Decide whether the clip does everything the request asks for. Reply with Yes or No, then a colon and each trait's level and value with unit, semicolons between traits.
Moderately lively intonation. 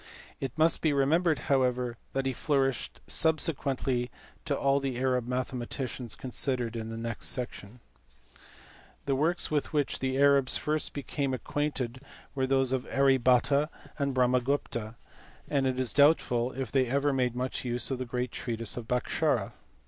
No: narrow, 2.2 semitones